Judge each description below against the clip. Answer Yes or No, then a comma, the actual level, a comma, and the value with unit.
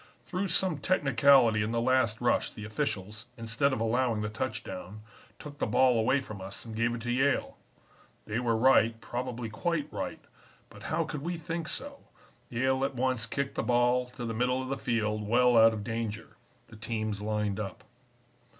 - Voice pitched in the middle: No, low, 120 Hz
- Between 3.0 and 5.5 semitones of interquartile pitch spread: Yes, average, 3.3 semitones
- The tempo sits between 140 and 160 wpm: No, average, 185 wpm